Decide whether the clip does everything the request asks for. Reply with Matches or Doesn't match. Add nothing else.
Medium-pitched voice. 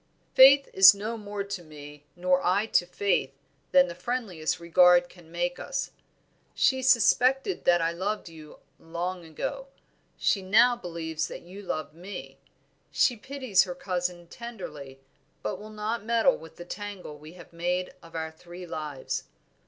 Matches